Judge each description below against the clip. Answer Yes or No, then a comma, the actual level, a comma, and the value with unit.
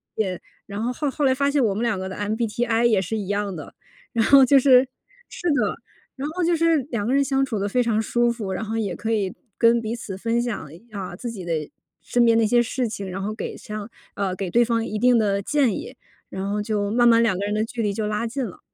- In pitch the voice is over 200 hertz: Yes, high, 225 Hz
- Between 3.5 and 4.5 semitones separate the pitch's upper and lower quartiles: No, average, 3.1 semitones